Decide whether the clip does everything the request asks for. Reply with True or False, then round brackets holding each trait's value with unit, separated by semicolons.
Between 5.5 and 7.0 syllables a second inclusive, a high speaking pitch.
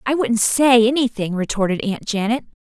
False (5.1 syllables/s; 230 Hz)